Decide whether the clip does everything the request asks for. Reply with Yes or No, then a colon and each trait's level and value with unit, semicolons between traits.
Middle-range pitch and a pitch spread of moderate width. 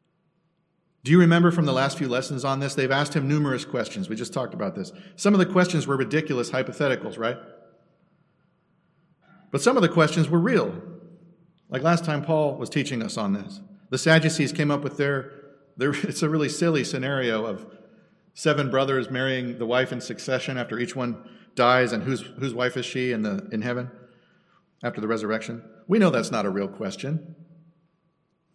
Yes: medium, 150 Hz; average, 4.8 semitones